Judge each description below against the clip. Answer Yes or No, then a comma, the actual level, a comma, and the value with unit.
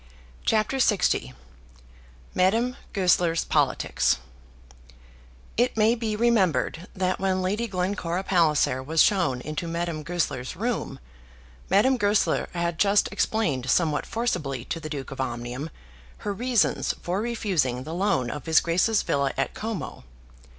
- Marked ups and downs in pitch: Yes, wide, 5.8 semitones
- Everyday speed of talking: No, slow, 130 wpm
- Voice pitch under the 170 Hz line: No, medium, 180 Hz